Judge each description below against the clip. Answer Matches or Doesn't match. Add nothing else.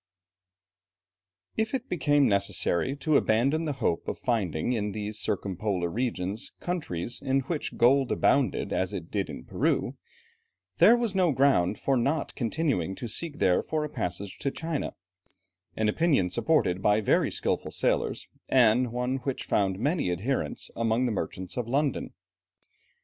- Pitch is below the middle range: Matches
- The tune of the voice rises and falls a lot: Matches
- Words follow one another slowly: Doesn't match